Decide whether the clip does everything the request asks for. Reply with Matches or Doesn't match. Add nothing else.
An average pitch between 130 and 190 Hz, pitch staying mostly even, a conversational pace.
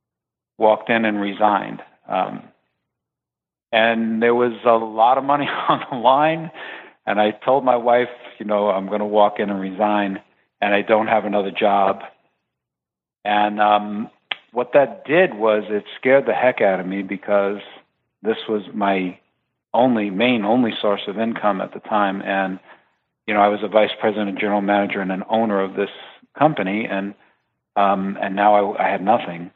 Doesn't match